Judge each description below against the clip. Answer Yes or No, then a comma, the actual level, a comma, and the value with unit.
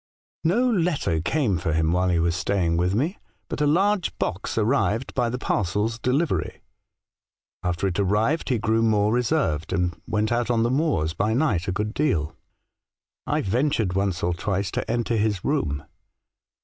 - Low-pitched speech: Yes, low, 105 Hz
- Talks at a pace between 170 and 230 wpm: Yes, average, 175 wpm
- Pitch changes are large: Yes, wide, 6.4 semitones